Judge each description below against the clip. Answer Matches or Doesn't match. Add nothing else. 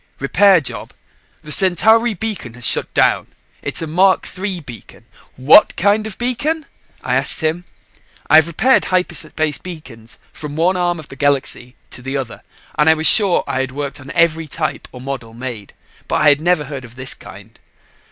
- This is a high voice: Doesn't match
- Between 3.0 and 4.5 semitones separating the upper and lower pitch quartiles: Doesn't match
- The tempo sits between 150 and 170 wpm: Doesn't match